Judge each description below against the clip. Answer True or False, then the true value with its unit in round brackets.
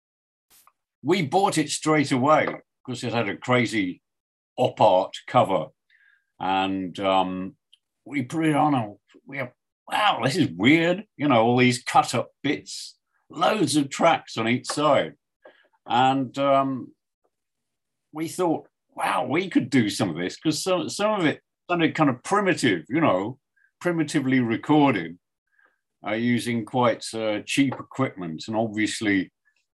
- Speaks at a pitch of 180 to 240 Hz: False (130 Hz)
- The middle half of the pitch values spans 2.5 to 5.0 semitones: False (5.6 semitones)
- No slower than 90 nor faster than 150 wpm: True (145 wpm)